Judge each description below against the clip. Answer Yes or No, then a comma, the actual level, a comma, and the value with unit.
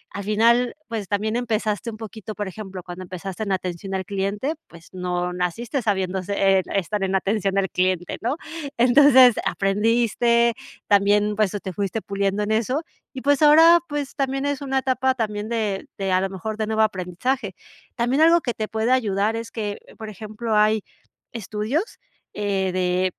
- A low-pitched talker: No, high, 210 Hz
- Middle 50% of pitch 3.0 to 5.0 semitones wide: Yes, average, 3.5 semitones